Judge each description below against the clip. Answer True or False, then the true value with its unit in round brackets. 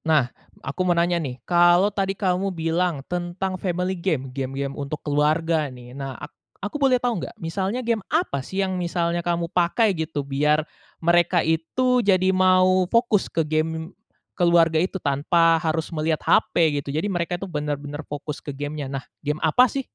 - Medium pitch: True (170 Hz)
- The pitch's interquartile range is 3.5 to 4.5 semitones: True (3.8 semitones)